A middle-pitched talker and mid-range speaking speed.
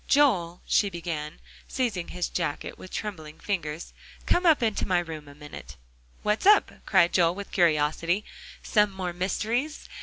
Yes: medium, 180 Hz; average, 150 wpm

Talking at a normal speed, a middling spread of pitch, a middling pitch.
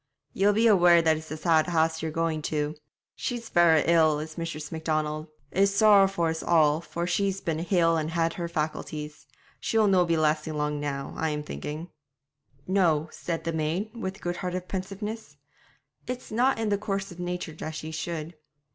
Yes: average, 180 wpm; average, 3.5 semitones; medium, 165 Hz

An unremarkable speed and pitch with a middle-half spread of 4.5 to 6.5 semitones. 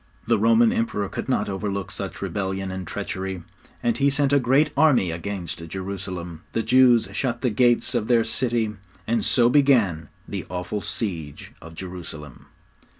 Yes: average, 155 wpm; average, 5.1 semitones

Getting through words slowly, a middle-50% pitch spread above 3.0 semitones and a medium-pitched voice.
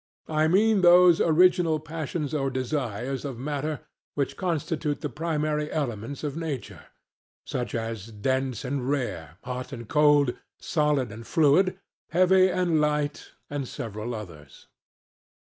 Yes: slow, 130 wpm; average, 4.2 semitones; medium, 145 Hz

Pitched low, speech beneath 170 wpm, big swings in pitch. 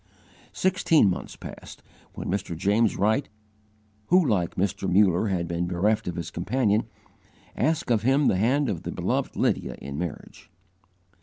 Yes: low, 105 Hz; average, 150 wpm; wide, 6.1 semitones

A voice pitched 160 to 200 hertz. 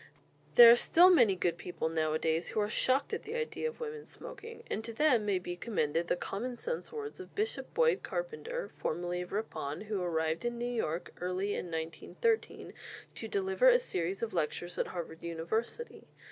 No: high, 215 Hz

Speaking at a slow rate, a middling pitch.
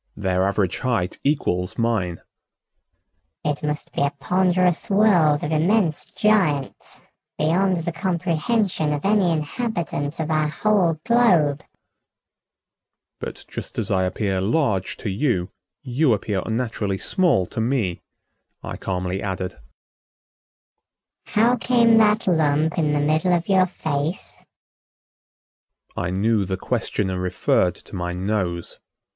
Yes: slow, 120 wpm; medium, 150 Hz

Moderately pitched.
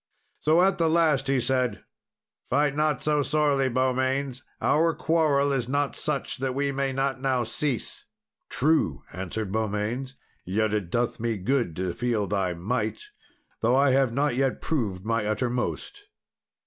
No: low, 130 Hz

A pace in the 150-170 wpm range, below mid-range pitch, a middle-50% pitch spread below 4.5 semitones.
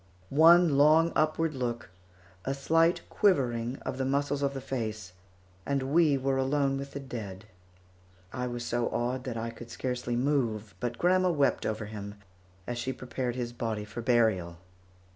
Yes: average, 160 wpm; low, 130 Hz; average, 3.2 semitones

